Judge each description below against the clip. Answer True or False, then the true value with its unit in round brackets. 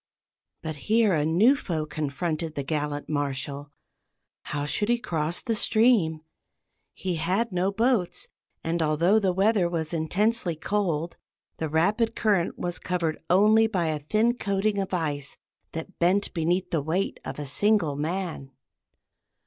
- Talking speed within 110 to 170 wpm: True (145 wpm)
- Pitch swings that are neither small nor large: True (4.7 semitones)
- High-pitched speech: False (175 Hz)